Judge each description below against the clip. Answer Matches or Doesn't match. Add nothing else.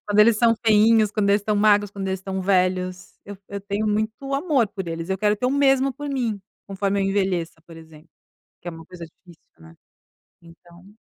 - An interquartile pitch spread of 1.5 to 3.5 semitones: Matches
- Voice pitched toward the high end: Matches